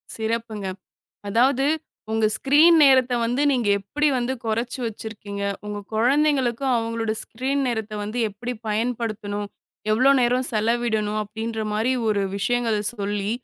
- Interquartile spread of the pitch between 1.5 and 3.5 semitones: Yes, average, 2.8 semitones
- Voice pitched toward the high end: Yes, high, 230 Hz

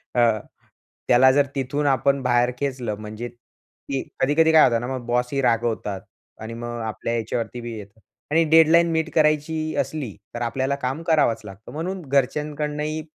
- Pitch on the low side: Yes, low, 130 Hz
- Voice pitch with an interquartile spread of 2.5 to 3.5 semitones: No, average, 4.3 semitones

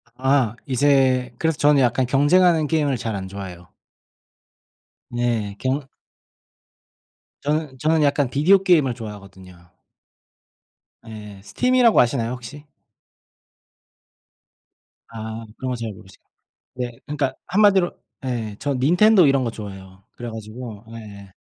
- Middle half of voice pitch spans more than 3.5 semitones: Yes, average, 5.1 semitones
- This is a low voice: Yes, low, 125 Hz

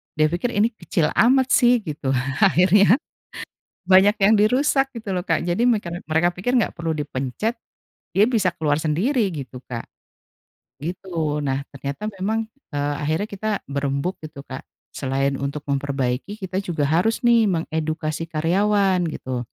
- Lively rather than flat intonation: Yes, wide, 6.2 semitones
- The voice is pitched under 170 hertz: No, medium, 175 Hz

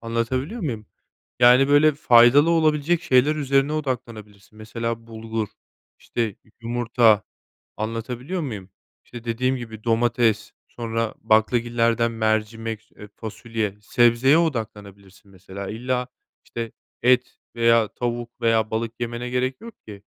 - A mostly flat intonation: Yes, narrow, 2.3 semitones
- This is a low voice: Yes, low, 115 Hz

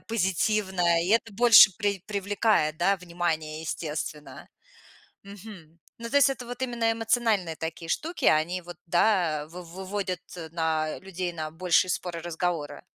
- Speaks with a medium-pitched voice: Yes, medium, 180 Hz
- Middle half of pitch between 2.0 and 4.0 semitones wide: No, average, 4.5 semitones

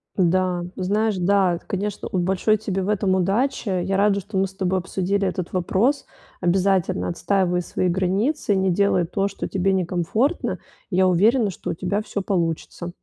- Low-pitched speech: No, high, 190 Hz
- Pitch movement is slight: Yes, narrow, 2.0 semitones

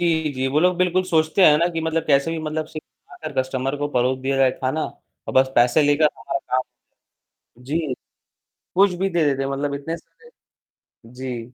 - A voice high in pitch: No, medium, 145 Hz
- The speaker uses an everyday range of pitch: Yes, average, 3.5 semitones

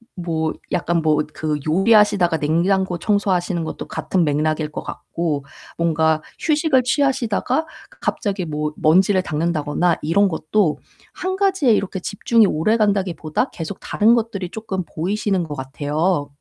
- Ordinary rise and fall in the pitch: Yes, average, 4.9 semitones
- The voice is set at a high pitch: No, medium, 180 Hz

